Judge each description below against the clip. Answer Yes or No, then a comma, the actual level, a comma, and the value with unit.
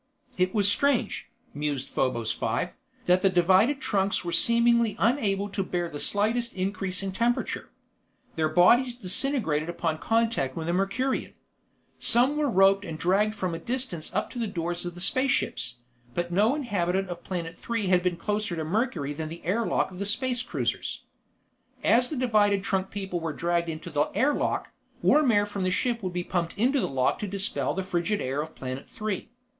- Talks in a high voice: Yes, high, 195 Hz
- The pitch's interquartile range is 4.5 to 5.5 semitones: Yes, average, 5.0 semitones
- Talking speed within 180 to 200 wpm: Yes, average, 190 wpm